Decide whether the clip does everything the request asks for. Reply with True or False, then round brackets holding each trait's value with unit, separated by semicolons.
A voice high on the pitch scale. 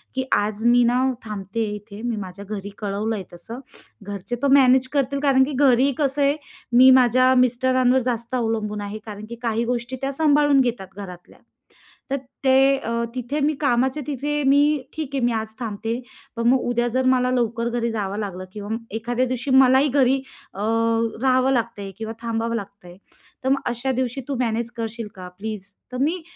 True (240 Hz)